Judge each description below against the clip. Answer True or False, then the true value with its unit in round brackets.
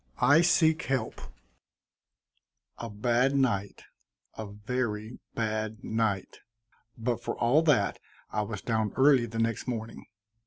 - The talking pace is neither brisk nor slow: False (120 wpm)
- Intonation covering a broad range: False (3.0 semitones)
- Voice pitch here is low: True (115 Hz)